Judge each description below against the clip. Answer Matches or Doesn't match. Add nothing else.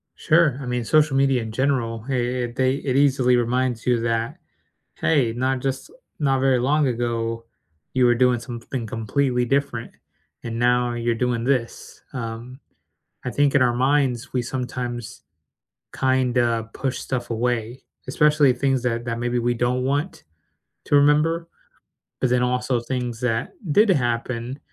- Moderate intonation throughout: Doesn't match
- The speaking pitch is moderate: Doesn't match